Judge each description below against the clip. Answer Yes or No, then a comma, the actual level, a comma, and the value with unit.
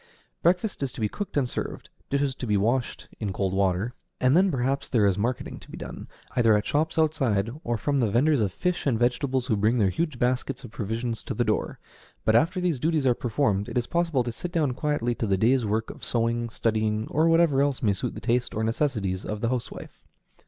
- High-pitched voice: No, low, 120 Hz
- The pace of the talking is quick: Yes, fast, 225 wpm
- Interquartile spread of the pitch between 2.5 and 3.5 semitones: No, average, 4.6 semitones